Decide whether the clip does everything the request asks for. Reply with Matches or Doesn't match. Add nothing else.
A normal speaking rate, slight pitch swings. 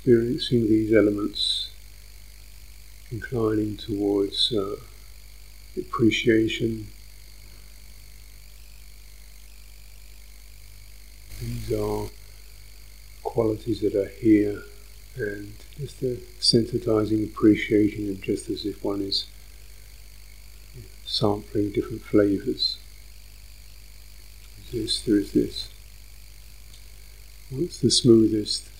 Doesn't match